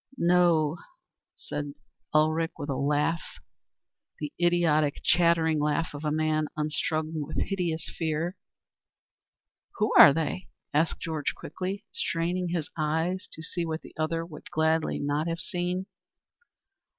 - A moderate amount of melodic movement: No, narrow, 2.0 semitones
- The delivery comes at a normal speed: No, slow, 125 wpm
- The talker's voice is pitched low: No, medium, 160 Hz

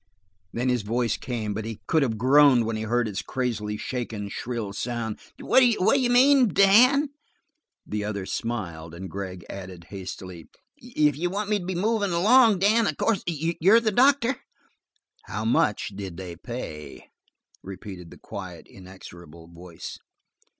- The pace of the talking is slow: No, average, 150 wpm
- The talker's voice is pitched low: Yes, low, 120 Hz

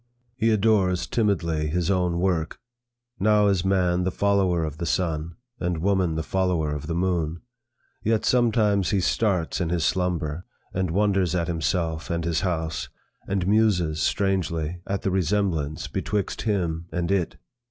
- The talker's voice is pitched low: Yes, very low, 90 Hz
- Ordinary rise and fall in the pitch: Yes, average, 3.1 semitones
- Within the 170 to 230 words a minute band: No, average, 150 wpm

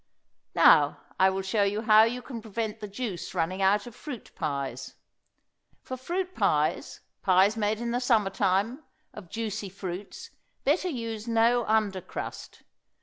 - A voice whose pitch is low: No, high, 215 Hz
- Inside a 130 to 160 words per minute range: Yes, average, 150 wpm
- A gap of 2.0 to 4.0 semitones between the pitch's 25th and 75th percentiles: Yes, average, 3.4 semitones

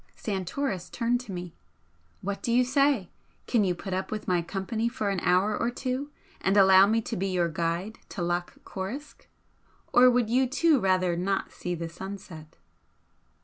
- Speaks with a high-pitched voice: Yes, high, 195 Hz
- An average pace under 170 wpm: No, average, 175 wpm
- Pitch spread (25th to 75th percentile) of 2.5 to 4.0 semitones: No, average, 4.8 semitones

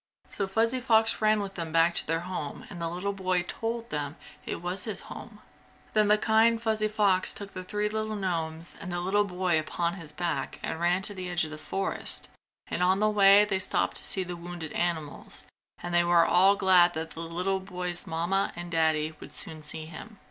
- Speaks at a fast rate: Yes, fast, 215 wpm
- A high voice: No, medium, 180 Hz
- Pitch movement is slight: No, average, 3.3 semitones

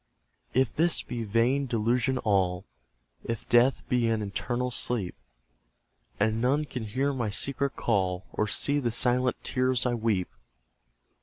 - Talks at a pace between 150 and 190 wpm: No, average, 140 wpm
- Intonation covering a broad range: No, average, 3.2 semitones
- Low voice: Yes, low, 120 Hz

